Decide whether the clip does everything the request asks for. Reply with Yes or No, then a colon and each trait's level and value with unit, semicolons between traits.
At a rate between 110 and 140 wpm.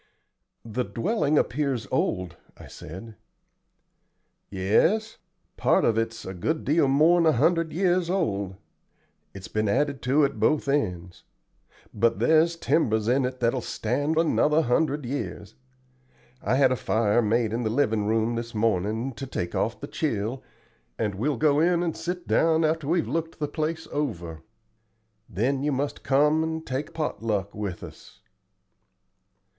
No: average, 150 wpm